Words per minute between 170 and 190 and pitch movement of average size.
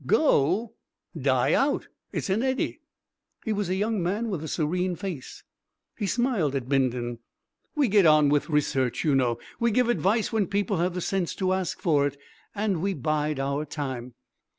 No: average, 175 wpm; wide, 6.1 semitones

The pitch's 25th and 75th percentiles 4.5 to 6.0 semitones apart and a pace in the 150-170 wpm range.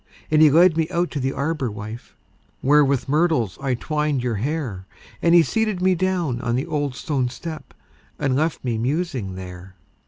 No: average, 5.0 semitones; average, 185 wpm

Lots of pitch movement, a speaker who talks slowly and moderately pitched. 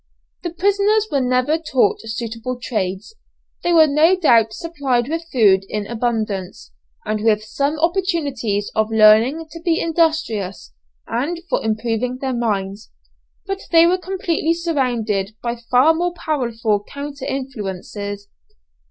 No: wide, 7.1 semitones; slow, 130 wpm; very high, 250 Hz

